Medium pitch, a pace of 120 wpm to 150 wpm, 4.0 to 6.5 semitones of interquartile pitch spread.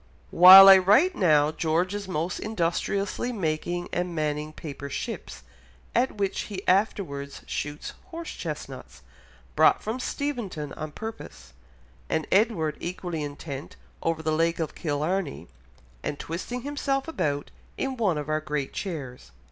Yes: medium, 175 Hz; slow, 135 wpm; average, 5.1 semitones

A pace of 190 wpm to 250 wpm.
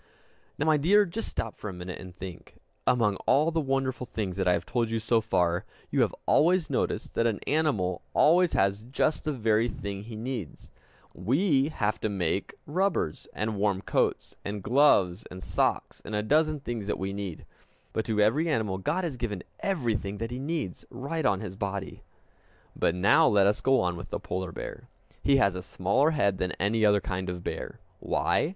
Yes: average, 195 wpm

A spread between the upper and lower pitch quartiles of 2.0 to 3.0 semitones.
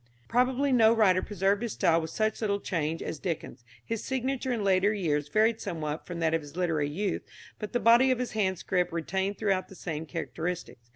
No: average, 5.2 semitones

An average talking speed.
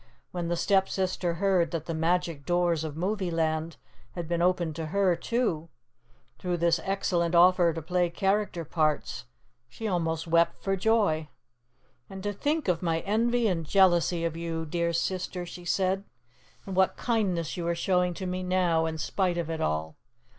Yes: average, 170 wpm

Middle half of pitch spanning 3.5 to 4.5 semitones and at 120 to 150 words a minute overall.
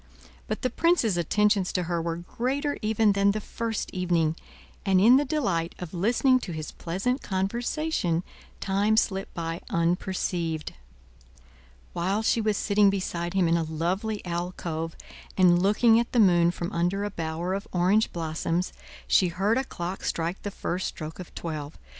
No: average, 3.9 semitones; average, 160 wpm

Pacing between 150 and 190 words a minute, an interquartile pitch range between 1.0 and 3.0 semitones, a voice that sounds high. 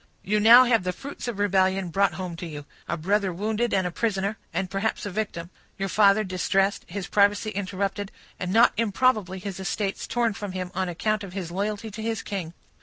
No: average, 200 wpm; narrow, 2.4 semitones; high, 200 Hz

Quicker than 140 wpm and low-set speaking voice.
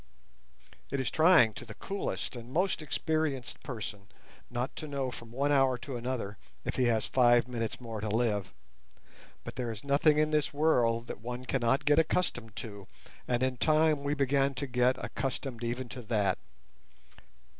Yes: average, 170 wpm; low, 125 Hz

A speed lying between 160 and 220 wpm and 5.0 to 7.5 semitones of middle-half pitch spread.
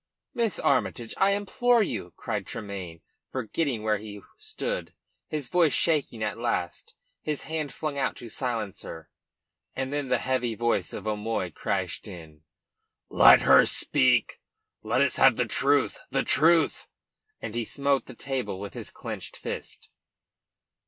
No: average, 145 wpm; wide, 5.5 semitones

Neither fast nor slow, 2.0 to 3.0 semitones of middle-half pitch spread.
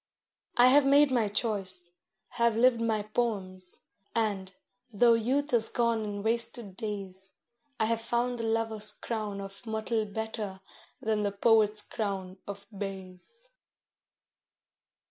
No: slow, 125 wpm; average, 2.7 semitones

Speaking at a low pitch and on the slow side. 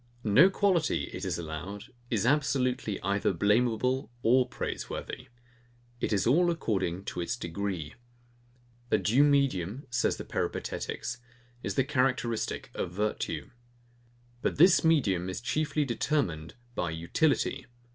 Yes: low, 120 Hz; slow, 125 wpm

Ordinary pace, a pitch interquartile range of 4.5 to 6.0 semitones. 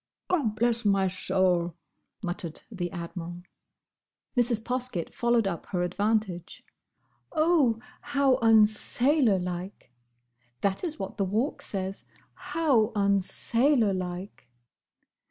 No: slow, 85 wpm; average, 5.1 semitones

